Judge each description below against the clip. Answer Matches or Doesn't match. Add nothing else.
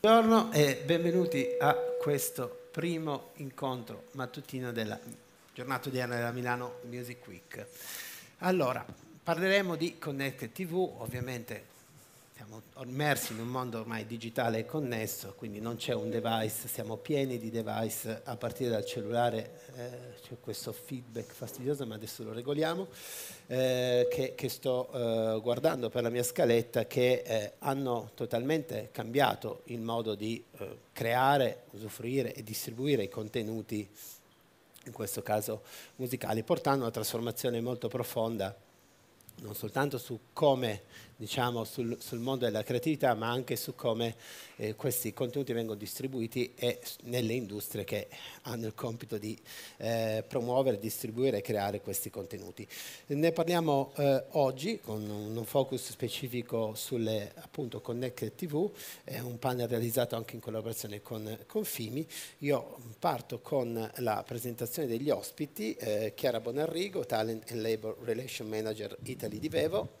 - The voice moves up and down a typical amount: Matches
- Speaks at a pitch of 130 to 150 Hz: Doesn't match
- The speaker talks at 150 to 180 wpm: Doesn't match